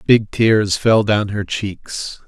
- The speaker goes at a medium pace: Yes, average, 160 wpm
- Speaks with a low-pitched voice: Yes, low, 105 Hz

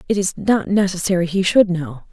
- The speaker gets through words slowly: No, average, 200 wpm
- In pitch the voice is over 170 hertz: Yes, medium, 185 Hz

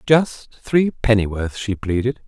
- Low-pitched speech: Yes, low, 115 Hz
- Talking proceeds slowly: Yes, slow, 105 wpm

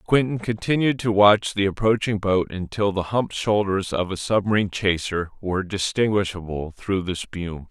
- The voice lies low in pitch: Yes, low, 100 Hz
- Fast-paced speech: No, average, 155 wpm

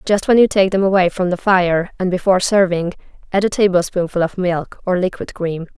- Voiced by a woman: Yes, female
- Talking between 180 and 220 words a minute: Yes, fast, 205 wpm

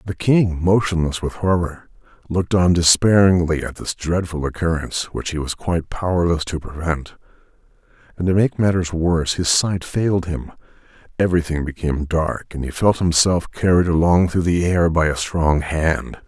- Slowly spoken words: No, average, 160 wpm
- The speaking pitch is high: No, very low, 85 Hz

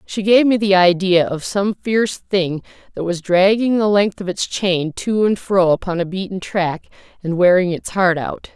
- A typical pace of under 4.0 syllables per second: No, 4.6 syllables/s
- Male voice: No, female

